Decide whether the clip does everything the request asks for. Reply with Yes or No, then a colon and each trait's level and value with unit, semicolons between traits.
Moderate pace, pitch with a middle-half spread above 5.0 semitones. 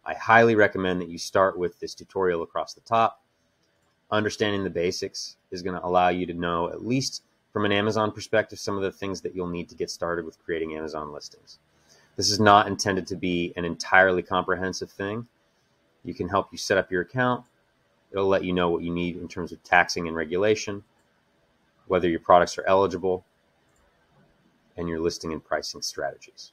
No: average, 190 wpm; average, 3.6 semitones